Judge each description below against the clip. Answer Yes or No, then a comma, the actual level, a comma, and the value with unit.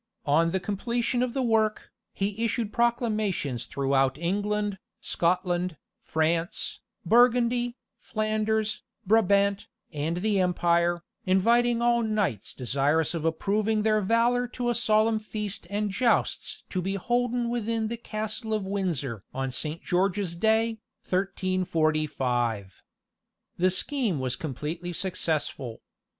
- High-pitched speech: Yes, high, 200 Hz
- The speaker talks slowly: Yes, slow, 115 wpm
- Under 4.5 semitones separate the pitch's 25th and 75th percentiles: No, average, 5.1 semitones